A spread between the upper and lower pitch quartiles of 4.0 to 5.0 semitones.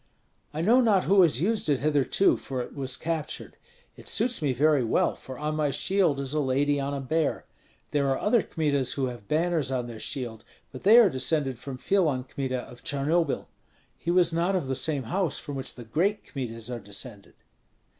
Yes: average, 4.5 semitones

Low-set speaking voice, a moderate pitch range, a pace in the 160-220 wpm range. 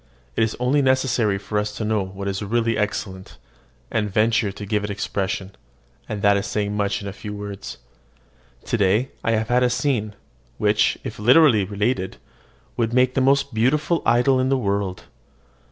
Yes: low, 105 Hz; average, 3.4 semitones; average, 175 wpm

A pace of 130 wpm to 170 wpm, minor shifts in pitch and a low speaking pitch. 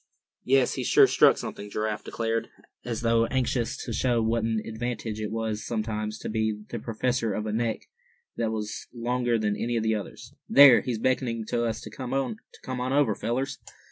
No: average, 185 wpm; narrow, 2.1 semitones; low, 115 Hz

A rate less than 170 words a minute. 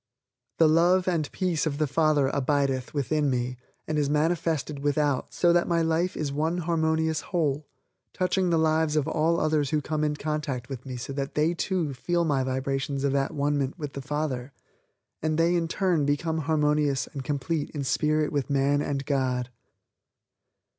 No: average, 180 wpm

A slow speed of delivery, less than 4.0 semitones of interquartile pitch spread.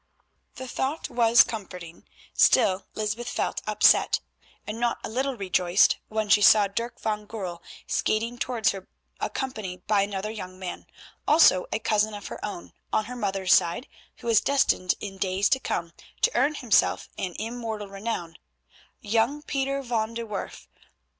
No: average, 155 wpm; average, 3.6 semitones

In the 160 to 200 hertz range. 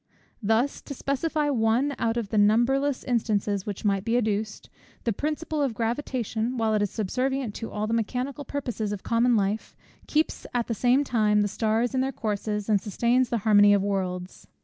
No: high, 225 Hz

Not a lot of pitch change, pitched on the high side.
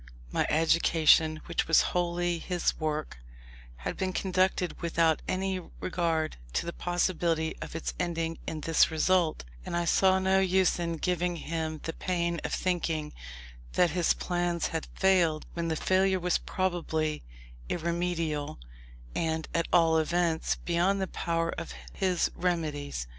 No: narrow, 1.9 semitones; medium, 170 Hz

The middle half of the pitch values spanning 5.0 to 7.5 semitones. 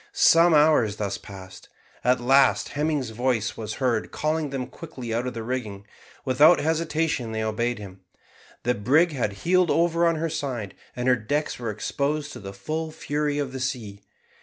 Yes: wide, 5.6 semitones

